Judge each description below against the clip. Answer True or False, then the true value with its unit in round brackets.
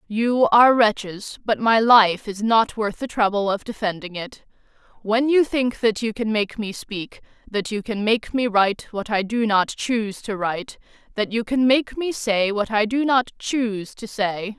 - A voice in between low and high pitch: False (220 Hz)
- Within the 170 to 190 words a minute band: False (200 wpm)